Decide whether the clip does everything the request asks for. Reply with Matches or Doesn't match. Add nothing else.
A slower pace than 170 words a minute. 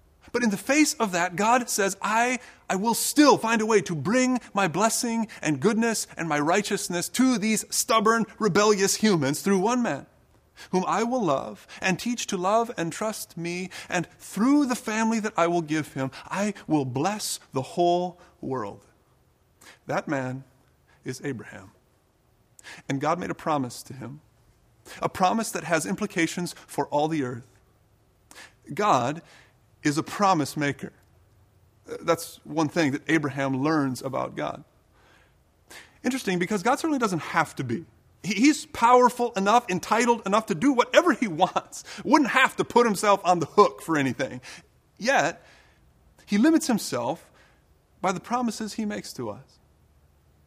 Matches